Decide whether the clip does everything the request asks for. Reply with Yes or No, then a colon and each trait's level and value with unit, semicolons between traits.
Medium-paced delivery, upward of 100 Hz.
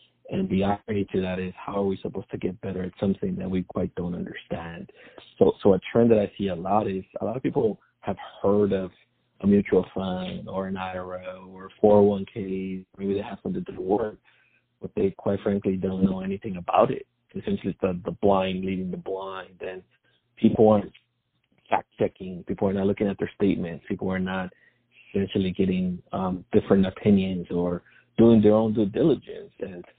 No: average, 190 wpm; very low, 95 Hz